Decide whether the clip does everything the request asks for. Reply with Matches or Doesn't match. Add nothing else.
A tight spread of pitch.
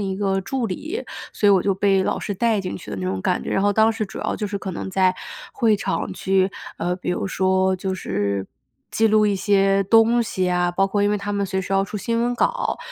Matches